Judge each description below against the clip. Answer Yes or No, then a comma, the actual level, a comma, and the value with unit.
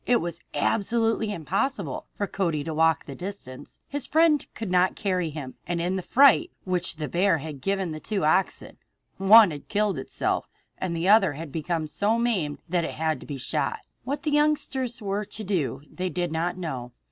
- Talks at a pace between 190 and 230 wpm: Yes, average, 195 wpm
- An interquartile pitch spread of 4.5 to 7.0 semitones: Yes, average, 5.1 semitones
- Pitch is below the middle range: No, medium, 180 Hz